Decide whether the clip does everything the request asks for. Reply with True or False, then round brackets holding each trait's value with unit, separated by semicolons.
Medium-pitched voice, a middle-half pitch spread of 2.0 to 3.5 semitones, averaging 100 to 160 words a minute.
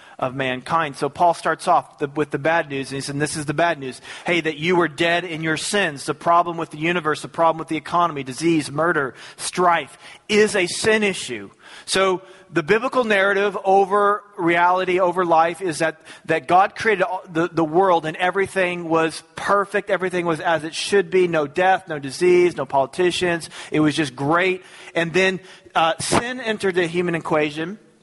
False (170 Hz; 2.7 semitones; 190 wpm)